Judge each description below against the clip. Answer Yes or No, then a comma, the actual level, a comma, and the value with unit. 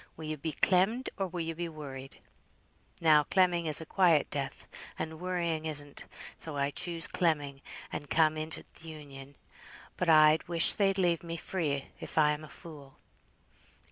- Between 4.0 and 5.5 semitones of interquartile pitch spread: No, narrow, 2.6 semitones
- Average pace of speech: Yes, average, 170 wpm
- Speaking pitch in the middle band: Yes, medium, 160 Hz